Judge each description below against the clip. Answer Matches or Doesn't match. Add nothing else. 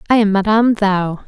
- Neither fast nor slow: Matches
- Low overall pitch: Doesn't match